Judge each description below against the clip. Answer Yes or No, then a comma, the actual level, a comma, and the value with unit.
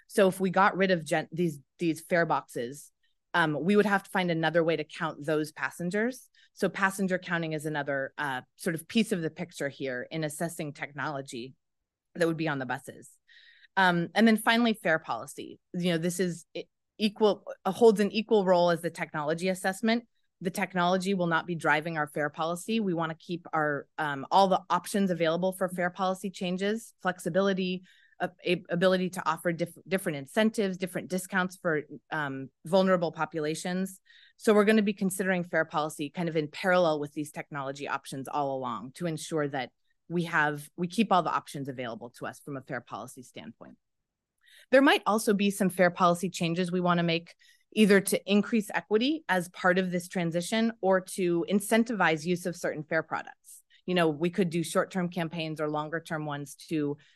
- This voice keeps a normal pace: Yes, average, 185 wpm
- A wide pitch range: No, average, 3.5 semitones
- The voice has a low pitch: No, medium, 175 Hz